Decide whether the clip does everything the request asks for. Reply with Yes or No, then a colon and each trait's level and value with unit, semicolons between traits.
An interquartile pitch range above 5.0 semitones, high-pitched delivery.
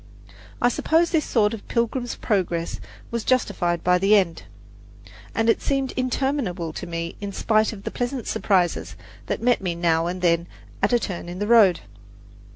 Yes: wide, 5.6 semitones; high, 205 Hz